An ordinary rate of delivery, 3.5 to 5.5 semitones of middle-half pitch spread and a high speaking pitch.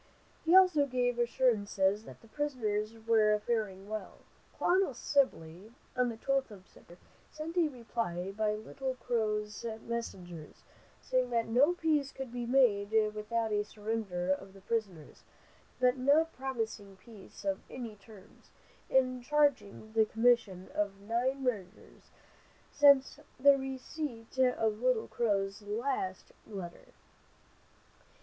No: slow, 125 wpm; average, 4.0 semitones; high, 225 Hz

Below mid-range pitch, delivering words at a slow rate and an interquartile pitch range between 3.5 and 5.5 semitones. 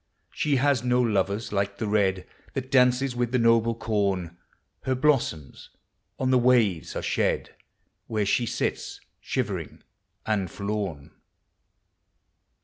Yes: low, 115 Hz; slow, 125 wpm; average, 4.0 semitones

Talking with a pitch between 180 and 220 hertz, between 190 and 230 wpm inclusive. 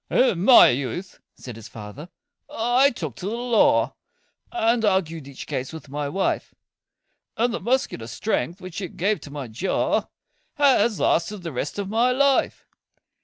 No: high, 190 Hz; average, 160 wpm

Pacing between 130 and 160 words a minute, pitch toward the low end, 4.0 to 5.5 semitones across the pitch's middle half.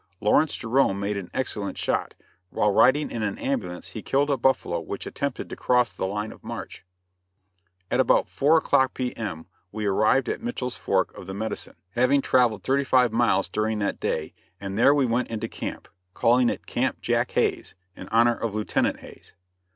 No: average, 180 wpm; low, 115 Hz; average, 4.3 semitones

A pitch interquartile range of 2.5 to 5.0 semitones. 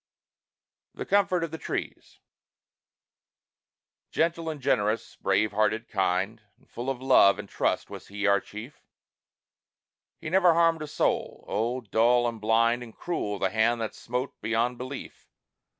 No: wide, 5.4 semitones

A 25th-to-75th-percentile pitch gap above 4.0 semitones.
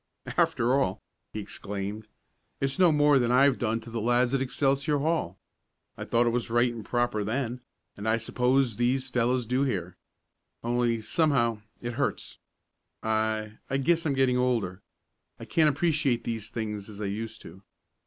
No: average, 3.5 semitones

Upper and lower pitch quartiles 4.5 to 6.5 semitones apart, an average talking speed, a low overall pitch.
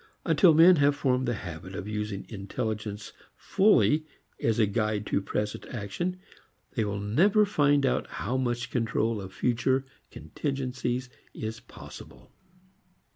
No: average, 5.2 semitones; slow, 130 wpm; low, 120 Hz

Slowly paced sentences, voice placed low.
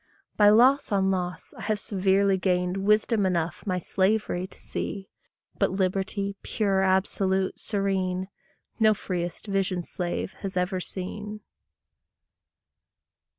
No: slow, 115 wpm; high, 190 Hz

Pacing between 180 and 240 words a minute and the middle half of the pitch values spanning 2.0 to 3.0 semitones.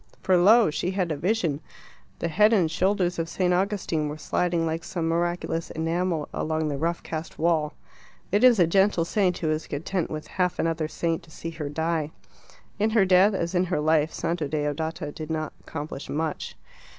Yes: average, 185 wpm; average, 2.7 semitones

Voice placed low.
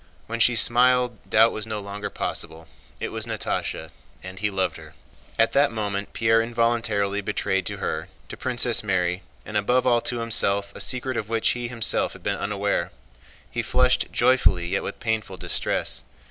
Yes: low, 110 Hz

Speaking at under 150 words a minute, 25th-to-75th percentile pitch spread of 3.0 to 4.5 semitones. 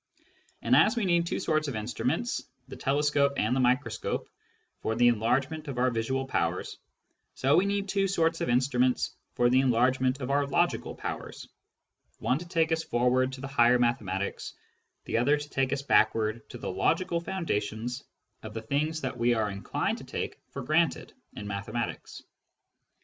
No: average, 170 wpm; average, 4.1 semitones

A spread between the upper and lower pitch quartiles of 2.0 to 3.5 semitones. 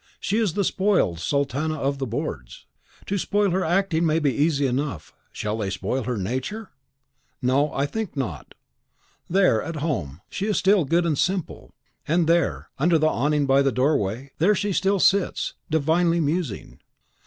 No: average, 5.3 semitones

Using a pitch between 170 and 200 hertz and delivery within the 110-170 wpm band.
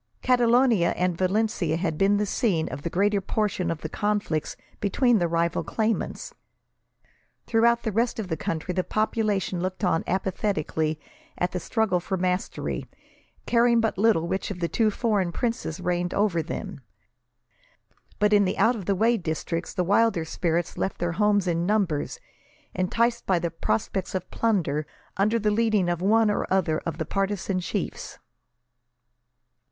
Yes: high, 190 Hz; average, 160 wpm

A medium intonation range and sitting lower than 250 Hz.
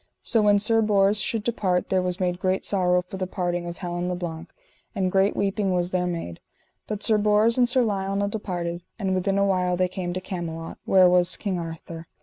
No: narrow, 2.2 semitones; medium, 185 Hz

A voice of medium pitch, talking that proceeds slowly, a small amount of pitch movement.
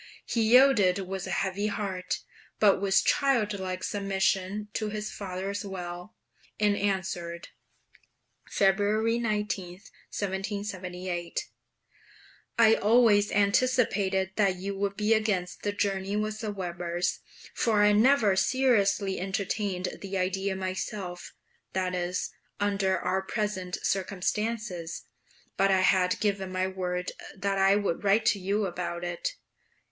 No: high, 195 Hz; slow, 120 wpm; narrow, 2.1 semitones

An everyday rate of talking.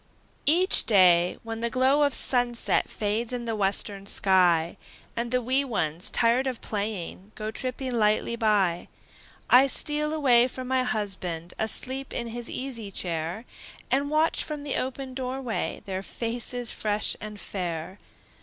Yes: average, 150 wpm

